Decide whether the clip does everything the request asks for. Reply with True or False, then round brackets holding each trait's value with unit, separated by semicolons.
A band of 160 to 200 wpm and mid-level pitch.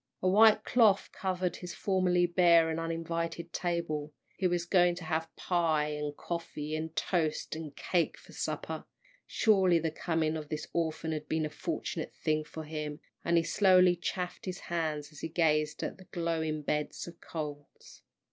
True (170 wpm; 165 Hz)